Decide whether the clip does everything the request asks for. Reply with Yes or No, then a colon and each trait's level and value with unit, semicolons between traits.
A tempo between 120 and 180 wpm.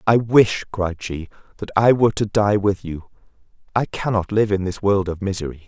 No: average, 200 wpm